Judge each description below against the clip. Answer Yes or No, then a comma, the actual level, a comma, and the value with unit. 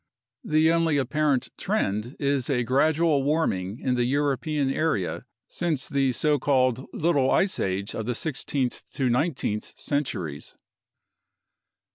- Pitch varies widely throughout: No, average, 3.8 semitones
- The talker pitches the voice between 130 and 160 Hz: Yes, low, 135 Hz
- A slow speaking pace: Yes, slow, 125 wpm